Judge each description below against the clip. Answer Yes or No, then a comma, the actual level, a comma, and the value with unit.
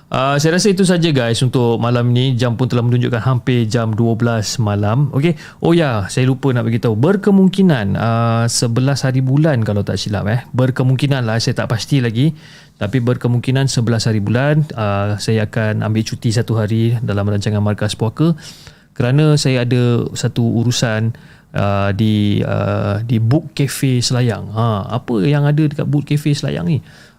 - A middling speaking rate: No, fast, 170 wpm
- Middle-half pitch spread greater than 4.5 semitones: No, average, 4.1 semitones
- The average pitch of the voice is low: Yes, low, 125 Hz